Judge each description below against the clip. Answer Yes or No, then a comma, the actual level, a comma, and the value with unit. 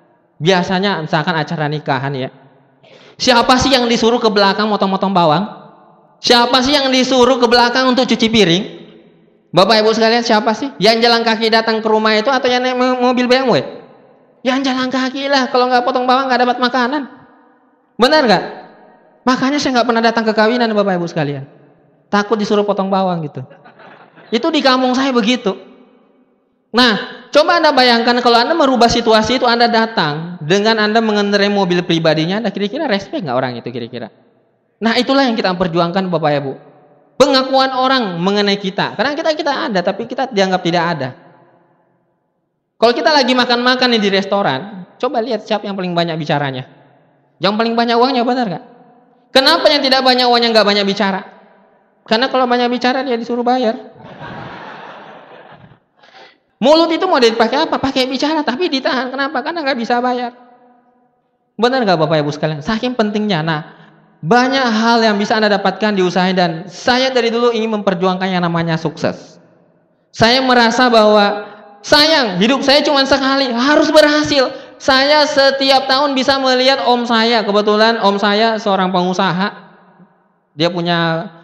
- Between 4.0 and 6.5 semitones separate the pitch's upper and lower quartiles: Yes, average, 5.0 semitones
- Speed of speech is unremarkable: No, fast, 155 wpm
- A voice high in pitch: Yes, high, 225 Hz